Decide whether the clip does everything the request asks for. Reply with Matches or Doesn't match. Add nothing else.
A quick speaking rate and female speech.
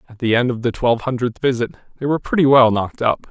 Doesn't match